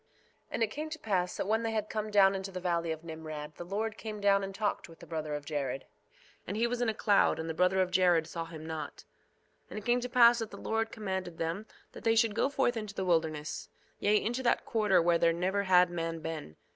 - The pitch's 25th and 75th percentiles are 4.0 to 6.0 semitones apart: Yes, average, 4.9 semitones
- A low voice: No, high, 190 Hz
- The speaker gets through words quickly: Yes, fast, 255 wpm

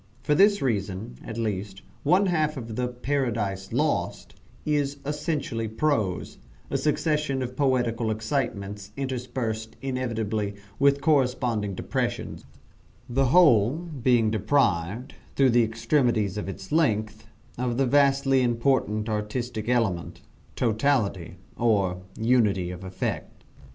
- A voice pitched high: No, low, 120 Hz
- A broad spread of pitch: No, average, 4.4 semitones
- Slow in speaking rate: Yes, slow, 115 wpm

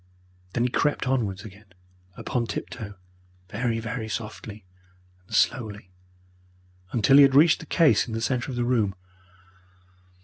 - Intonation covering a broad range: No, average, 3.3 semitones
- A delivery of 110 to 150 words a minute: Yes, average, 140 wpm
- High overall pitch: No, low, 115 Hz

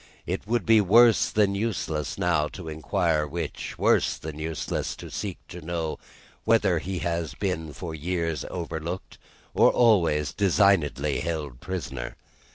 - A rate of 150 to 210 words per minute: No, average, 140 wpm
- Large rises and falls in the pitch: No, average, 3.8 semitones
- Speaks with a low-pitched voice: Yes, very low, 85 Hz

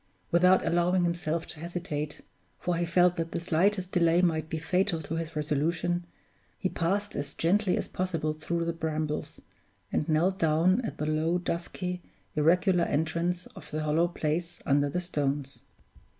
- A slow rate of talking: No, average, 160 wpm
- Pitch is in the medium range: Yes, medium, 170 Hz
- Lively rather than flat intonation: No, narrow, 2.5 semitones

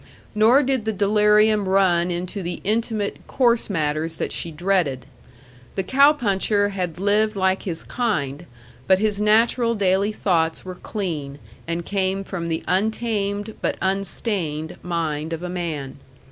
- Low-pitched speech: No, high, 195 Hz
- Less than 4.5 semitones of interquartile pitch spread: Yes, average, 3.9 semitones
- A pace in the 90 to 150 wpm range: Yes, average, 145 wpm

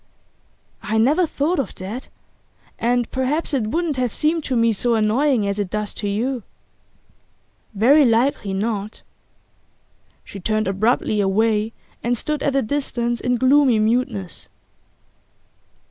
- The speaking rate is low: Yes, slow, 130 wpm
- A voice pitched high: Yes, high, 235 Hz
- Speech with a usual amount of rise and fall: Yes, average, 4.1 semitones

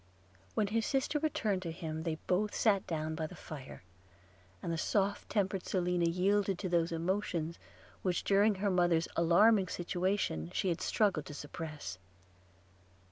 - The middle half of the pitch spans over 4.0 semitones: No, average, 3.7 semitones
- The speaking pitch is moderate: Yes, medium, 180 Hz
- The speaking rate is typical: Yes, average, 150 wpm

